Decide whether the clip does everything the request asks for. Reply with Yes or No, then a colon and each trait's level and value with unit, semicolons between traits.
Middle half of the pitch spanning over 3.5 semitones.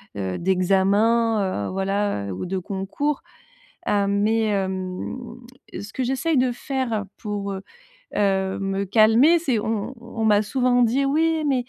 Yes: average, 4.3 semitones